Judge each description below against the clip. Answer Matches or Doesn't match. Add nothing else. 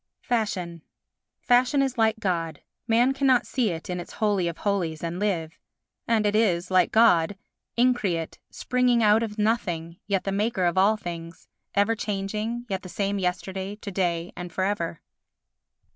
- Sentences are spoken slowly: Doesn't match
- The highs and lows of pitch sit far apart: Doesn't match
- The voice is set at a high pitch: Matches